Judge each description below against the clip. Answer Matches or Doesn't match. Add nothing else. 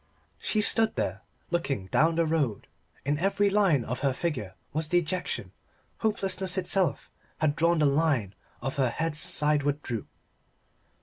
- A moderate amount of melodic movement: Matches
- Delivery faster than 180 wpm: Doesn't match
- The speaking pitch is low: Doesn't match